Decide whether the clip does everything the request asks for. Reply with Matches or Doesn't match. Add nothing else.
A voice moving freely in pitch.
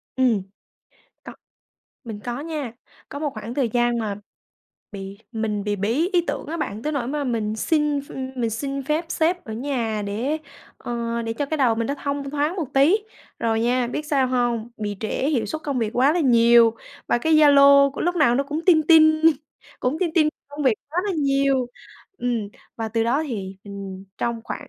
Doesn't match